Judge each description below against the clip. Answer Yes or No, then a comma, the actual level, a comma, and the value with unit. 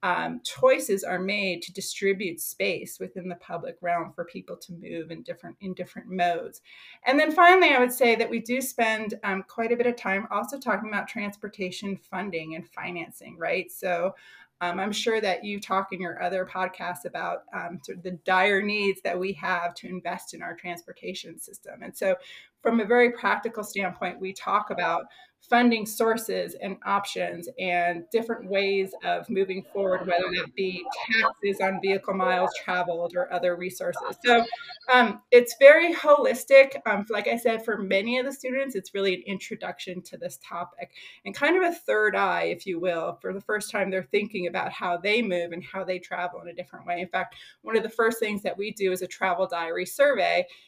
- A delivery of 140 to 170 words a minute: No, average, 195 wpm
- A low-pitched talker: No, high, 195 Hz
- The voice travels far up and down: No, average, 4.1 semitones